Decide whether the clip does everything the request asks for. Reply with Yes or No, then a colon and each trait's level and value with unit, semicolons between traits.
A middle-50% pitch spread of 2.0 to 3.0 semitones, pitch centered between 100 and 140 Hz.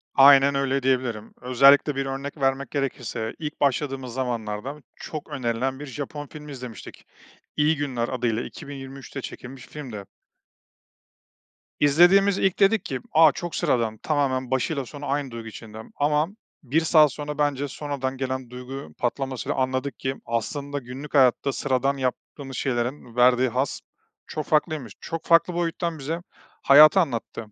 Yes: narrow, 2.6 semitones; low, 135 Hz